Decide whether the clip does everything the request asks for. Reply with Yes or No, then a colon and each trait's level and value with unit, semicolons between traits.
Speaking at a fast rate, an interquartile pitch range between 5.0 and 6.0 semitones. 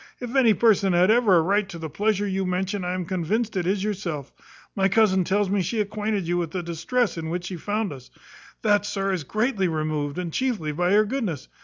No: fast, 225 wpm; average, 3.4 semitones